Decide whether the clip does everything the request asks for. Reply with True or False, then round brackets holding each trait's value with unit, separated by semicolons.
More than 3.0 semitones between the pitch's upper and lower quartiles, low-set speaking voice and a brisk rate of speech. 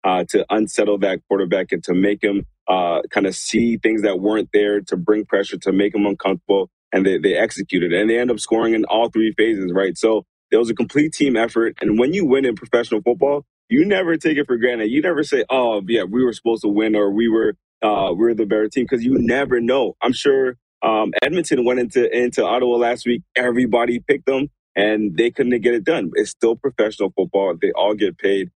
False (2.7 semitones; 115 Hz; 225 wpm)